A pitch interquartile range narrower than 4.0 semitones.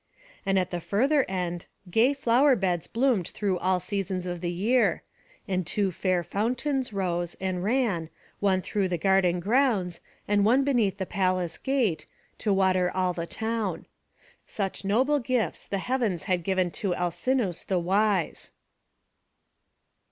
No: average, 4.3 semitones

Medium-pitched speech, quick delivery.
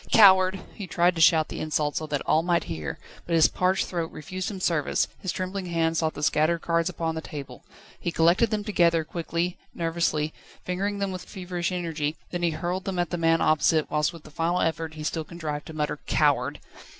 Yes: medium, 170 Hz; fast, 210 wpm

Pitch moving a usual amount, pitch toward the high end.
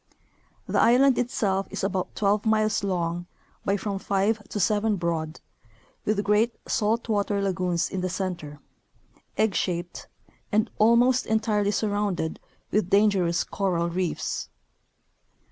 Yes: average, 3.0 semitones; high, 200 Hz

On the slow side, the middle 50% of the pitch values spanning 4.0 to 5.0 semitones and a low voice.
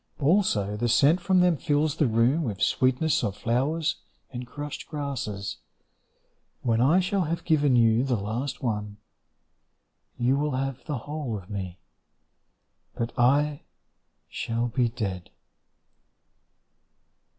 Yes: slow, 125 wpm; average, 4.7 semitones; low, 130 Hz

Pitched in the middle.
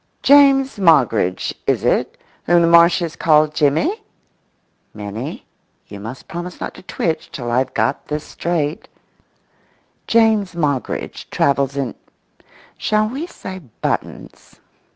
Yes: medium, 160 Hz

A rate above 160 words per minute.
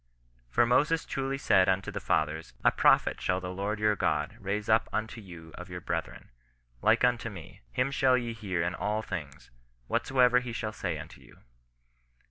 Yes: average, 180 wpm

